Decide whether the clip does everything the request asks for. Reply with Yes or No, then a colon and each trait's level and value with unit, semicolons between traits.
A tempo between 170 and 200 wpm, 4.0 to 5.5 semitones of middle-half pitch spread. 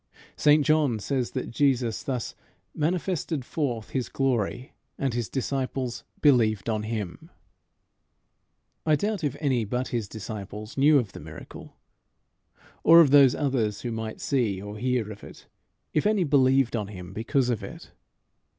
No: average, 150 wpm; average, 4.4 semitones